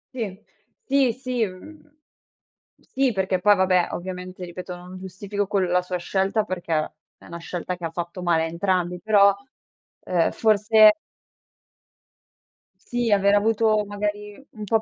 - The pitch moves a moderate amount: Yes, average, 3.0 semitones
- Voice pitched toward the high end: Yes, high, 195 Hz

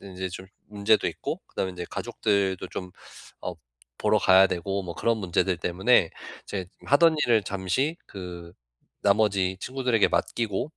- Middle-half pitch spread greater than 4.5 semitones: No, average, 3.2 semitones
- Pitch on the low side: Yes, very low, 95 Hz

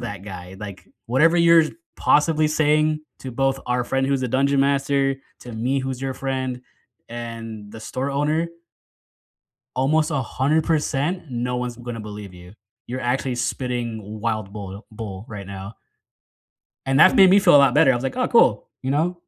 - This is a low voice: Yes, low, 130 Hz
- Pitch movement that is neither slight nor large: Yes, average, 4.3 semitones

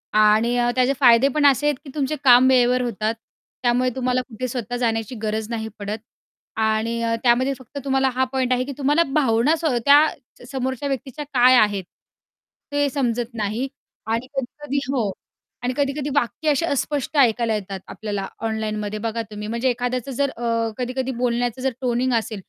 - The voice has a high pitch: Yes, high, 245 Hz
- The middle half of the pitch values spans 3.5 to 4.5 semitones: No, average, 3.0 semitones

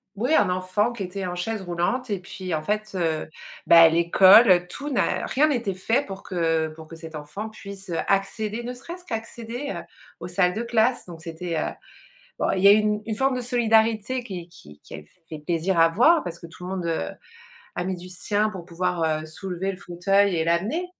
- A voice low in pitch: No, high, 190 Hz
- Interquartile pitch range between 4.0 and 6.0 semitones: Yes, average, 4.5 semitones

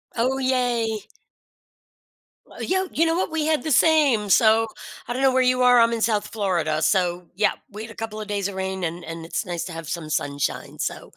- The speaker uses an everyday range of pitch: No, wide, 5.7 semitones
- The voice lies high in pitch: Yes, high, 220 Hz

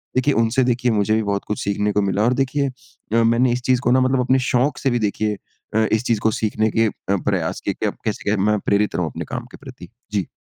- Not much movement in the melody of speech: No, average, 3.3 semitones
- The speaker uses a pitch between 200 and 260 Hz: No, low, 110 Hz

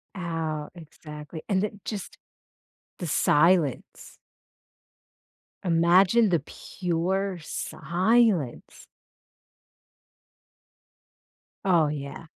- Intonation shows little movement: No, average, 3.7 semitones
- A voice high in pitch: No, medium, 170 Hz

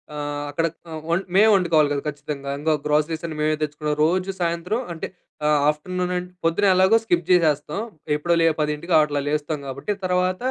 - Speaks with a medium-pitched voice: Yes, medium, 160 Hz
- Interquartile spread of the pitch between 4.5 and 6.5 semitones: No, average, 3.3 semitones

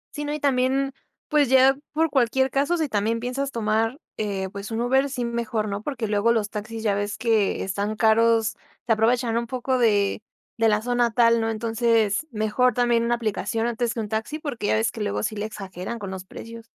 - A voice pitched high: Yes, high, 230 Hz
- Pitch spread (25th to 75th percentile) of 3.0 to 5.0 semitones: No, narrow, 2.6 semitones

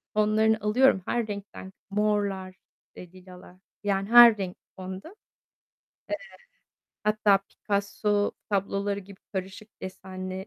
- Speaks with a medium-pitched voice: No, high, 200 Hz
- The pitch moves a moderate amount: No, narrow, 2.0 semitones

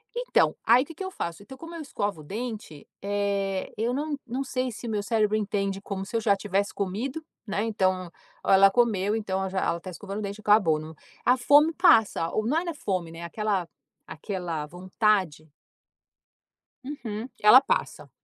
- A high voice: Yes, high, 205 Hz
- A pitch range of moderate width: Yes, average, 4.2 semitones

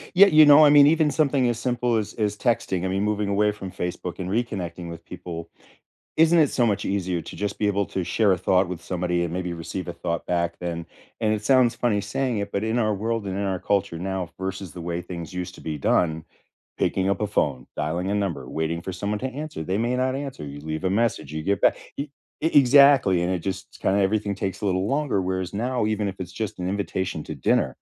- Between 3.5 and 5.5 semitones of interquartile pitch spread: Yes, average, 4.3 semitones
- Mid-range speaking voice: No, low, 100 Hz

